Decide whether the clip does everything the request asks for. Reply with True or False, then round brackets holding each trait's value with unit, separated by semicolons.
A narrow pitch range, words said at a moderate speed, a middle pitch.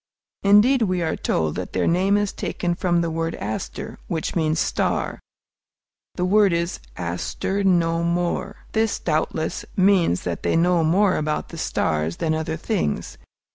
False (3.3 semitones; 155 wpm; 170 Hz)